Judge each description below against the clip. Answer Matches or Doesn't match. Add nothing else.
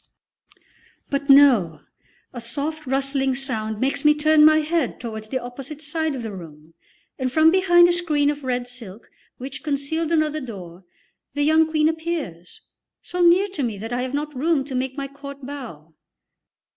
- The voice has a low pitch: Doesn't match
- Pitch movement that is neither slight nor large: Matches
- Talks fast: Doesn't match